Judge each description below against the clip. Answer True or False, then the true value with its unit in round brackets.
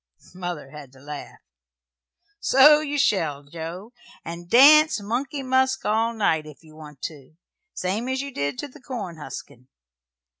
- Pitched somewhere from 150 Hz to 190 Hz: True (185 Hz)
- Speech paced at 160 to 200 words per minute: False (150 wpm)